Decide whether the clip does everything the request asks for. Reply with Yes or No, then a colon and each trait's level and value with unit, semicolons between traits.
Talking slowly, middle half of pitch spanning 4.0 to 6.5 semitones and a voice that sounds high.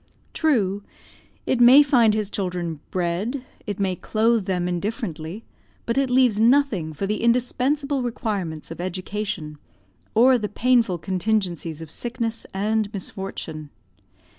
Yes: slow, 125 wpm; average, 5.0 semitones; high, 210 Hz